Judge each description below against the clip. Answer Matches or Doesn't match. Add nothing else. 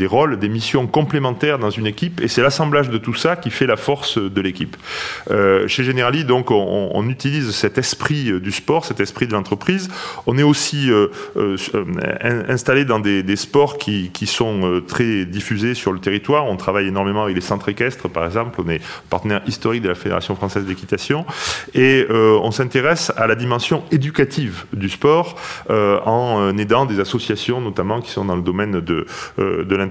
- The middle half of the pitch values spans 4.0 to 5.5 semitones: Matches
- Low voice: Matches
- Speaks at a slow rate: Doesn't match